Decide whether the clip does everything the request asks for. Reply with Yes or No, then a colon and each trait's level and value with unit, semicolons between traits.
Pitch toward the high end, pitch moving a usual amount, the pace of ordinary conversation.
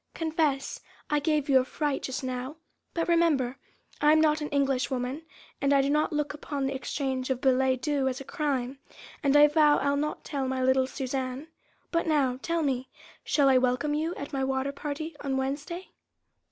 No: very high, 280 Hz; narrow, 2.3 semitones; average, 190 wpm